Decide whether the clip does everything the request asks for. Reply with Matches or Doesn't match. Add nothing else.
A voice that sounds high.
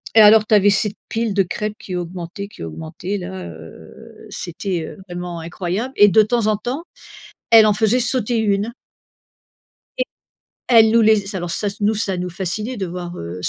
Matches